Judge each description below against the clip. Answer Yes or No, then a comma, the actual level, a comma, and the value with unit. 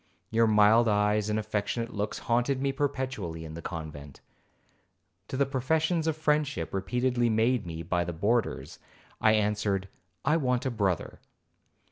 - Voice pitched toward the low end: Yes, low, 110 Hz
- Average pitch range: Yes, average, 4.5 semitones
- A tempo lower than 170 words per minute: Yes, average, 145 wpm